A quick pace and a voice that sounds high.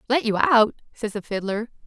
No: average, 195 wpm; high, 225 Hz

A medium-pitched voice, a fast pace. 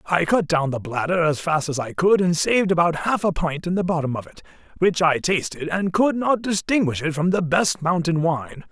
Yes: medium, 170 Hz; fast, 235 wpm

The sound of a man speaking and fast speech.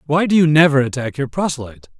Yes: male; fast, 210 wpm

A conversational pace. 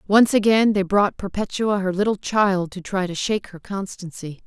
Yes: average, 190 wpm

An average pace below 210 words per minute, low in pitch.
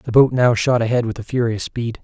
No: fast, 235 wpm; low, 120 Hz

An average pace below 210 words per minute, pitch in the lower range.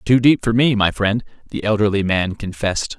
Yes: average, 200 wpm; low, 105 Hz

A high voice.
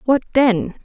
Yes: high, 240 Hz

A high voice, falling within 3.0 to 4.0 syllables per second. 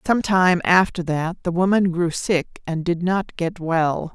No: medium, 175 Hz; 3.9 syllables/s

